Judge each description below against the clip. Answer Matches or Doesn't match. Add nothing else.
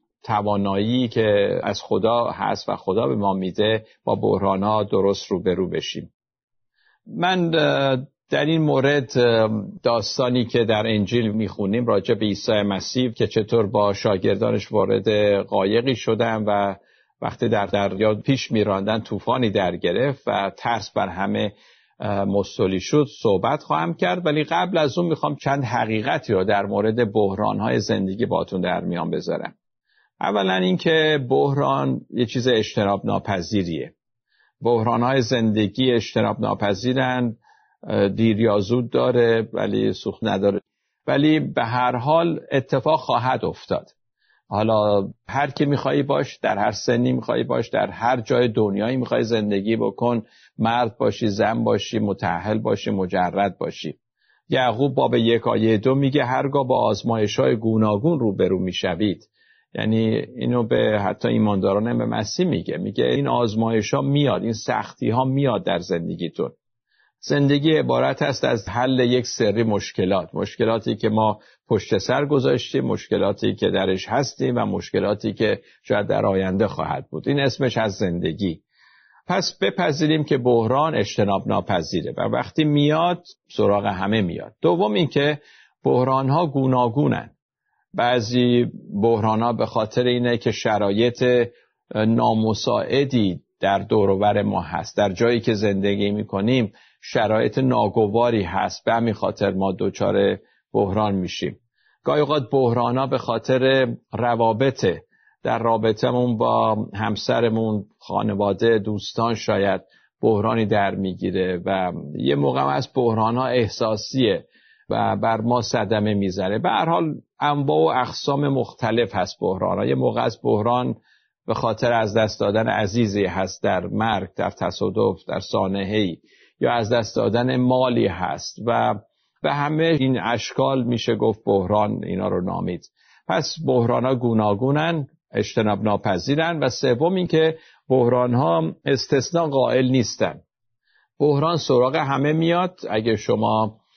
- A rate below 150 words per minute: Matches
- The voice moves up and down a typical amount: Matches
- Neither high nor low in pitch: Doesn't match